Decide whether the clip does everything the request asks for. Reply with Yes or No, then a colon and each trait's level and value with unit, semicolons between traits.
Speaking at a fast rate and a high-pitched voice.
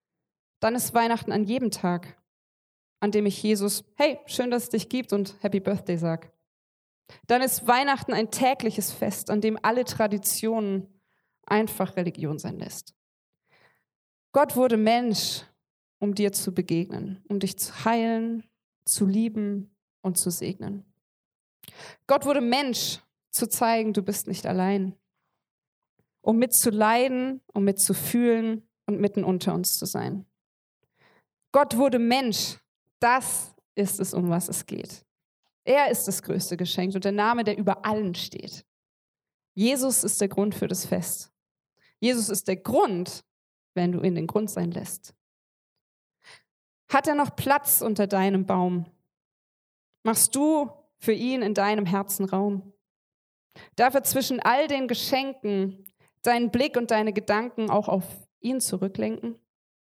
No: average, 140 wpm; high, 205 Hz